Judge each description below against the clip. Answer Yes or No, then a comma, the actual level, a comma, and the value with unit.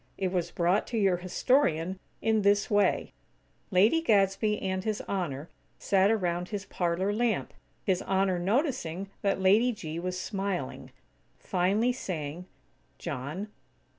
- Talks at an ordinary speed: No, slow, 130 wpm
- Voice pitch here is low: No, high, 190 Hz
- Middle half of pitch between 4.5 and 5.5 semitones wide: No, average, 2.9 semitones